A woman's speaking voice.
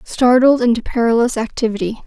Yes: female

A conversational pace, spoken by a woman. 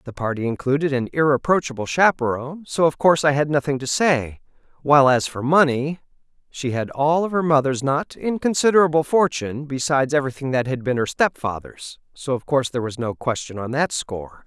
No: average, 180 wpm; male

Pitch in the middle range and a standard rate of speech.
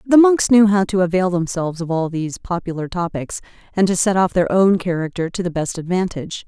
No: medium, 180 Hz; fast, 215 wpm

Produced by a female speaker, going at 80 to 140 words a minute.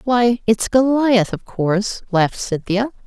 Yes: female; slow, 135 wpm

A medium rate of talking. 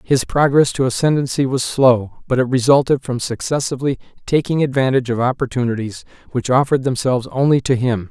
Yes: average, 155 wpm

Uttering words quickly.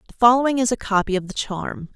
Yes: fast, 245 wpm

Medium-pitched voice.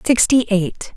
No: high, 220 Hz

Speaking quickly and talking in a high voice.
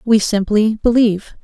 No: slow, 125 wpm; high, 215 Hz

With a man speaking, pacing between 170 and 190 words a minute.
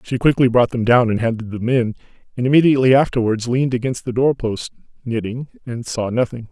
Yes: male; average, 185 wpm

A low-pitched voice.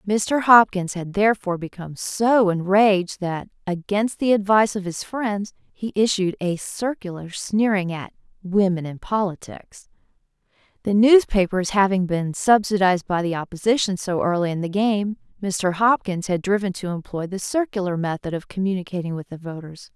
No: high, 195 Hz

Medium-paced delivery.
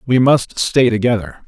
Yes: average, 165 wpm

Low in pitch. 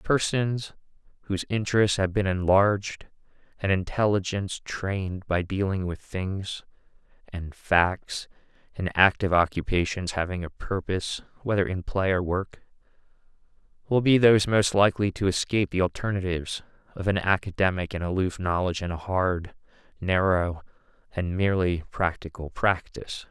Yes: very low, 95 Hz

